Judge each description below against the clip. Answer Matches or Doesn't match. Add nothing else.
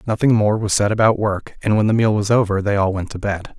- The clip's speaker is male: Matches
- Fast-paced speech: Matches